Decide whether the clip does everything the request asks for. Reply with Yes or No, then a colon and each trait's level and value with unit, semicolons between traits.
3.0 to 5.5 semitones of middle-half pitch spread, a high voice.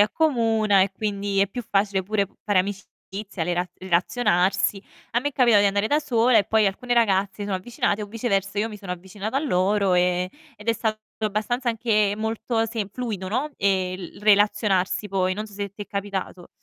No: narrow, 2.4 semitones; high, 205 Hz